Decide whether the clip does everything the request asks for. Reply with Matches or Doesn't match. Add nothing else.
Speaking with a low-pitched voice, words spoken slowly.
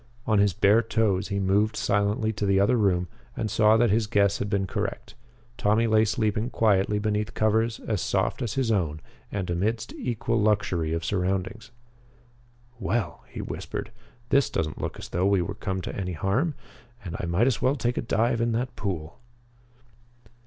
Doesn't match